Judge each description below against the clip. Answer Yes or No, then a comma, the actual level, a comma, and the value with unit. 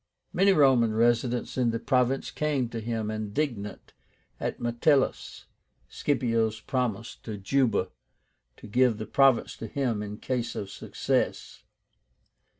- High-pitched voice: No, low, 120 Hz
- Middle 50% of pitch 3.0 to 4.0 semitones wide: Yes, average, 3.3 semitones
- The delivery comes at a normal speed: No, slow, 125 wpm